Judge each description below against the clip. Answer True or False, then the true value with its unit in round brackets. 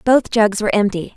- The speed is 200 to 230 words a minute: True (205 wpm)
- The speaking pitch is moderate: False (215 Hz)